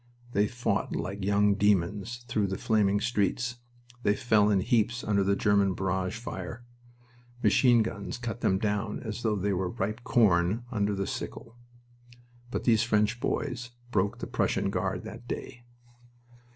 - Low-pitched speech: Yes, low, 105 Hz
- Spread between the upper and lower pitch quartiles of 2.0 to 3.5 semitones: Yes, average, 2.9 semitones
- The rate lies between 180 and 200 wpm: No, average, 150 wpm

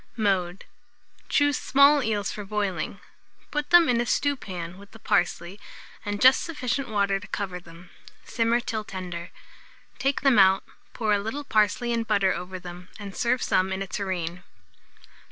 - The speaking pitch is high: Yes, high, 205 Hz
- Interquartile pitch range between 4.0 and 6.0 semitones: Yes, average, 4.5 semitones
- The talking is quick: No, average, 160 wpm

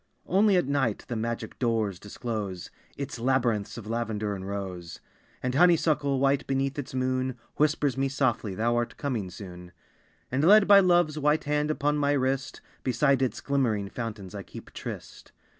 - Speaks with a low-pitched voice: Yes, low, 130 Hz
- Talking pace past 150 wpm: Yes, average, 160 wpm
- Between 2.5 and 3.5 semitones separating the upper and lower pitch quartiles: No, average, 4.7 semitones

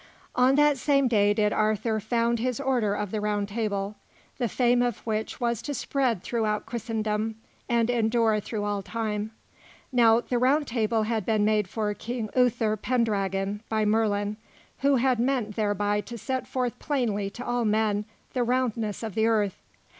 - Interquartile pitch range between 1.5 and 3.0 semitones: Yes, average, 2.7 semitones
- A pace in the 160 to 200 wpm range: Yes, average, 170 wpm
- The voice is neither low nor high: No, high, 225 Hz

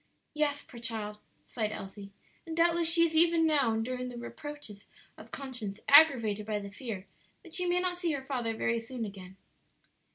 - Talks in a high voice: Yes, very high, 250 Hz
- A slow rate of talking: No, average, 175 wpm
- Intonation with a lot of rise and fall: Yes, wide, 6.8 semitones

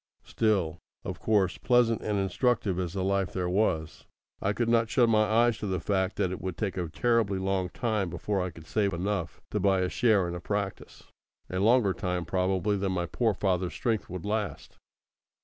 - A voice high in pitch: No, very low, 95 Hz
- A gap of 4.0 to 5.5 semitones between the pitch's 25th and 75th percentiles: No, average, 2.9 semitones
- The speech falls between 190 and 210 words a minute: Yes, average, 200 wpm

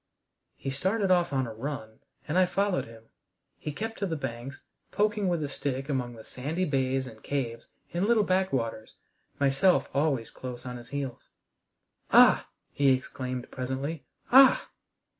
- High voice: No, medium, 140 Hz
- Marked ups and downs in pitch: Yes, wide, 5.9 semitones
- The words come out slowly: No, average, 160 wpm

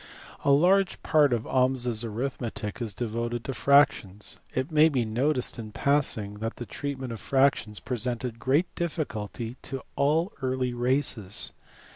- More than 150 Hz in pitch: No, low, 125 Hz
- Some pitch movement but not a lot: Yes, average, 3.5 semitones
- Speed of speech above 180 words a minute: No, average, 145 wpm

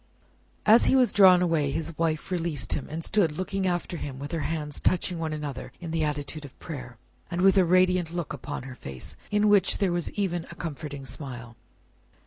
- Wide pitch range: No, average, 3.9 semitones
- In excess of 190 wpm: Yes, average, 200 wpm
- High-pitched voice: No, medium, 165 Hz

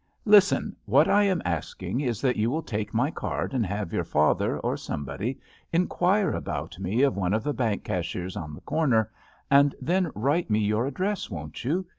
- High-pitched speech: No, low, 120 Hz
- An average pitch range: No, wide, 8.2 semitones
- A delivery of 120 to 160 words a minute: No, fast, 205 wpm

